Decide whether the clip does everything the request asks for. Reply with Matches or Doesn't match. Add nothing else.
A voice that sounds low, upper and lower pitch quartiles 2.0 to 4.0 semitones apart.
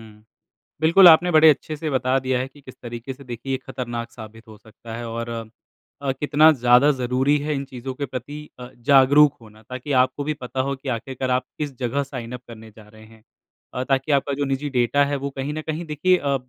Matches